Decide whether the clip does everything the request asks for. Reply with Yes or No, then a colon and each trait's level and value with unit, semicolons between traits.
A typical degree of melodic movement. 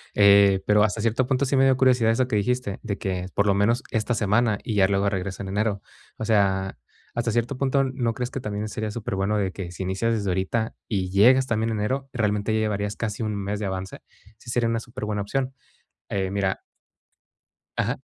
Yes: average, 3.0 semitones